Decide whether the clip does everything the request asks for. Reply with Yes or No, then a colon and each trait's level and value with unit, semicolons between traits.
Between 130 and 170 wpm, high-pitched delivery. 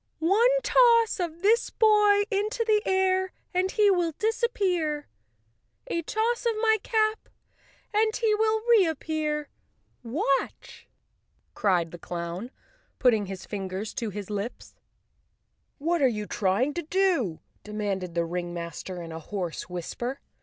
Yes: average, 140 wpm; very high, 315 Hz